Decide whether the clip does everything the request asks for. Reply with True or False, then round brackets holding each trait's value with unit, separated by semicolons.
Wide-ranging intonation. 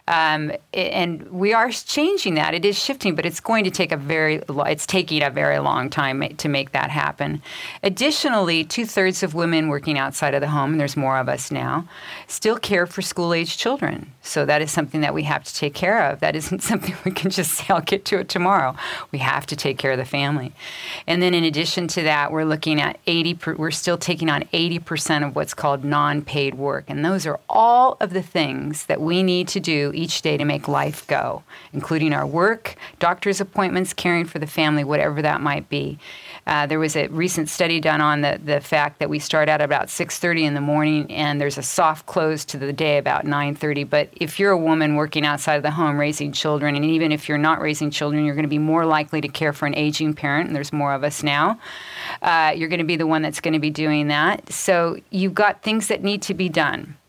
False (3.0 semitones)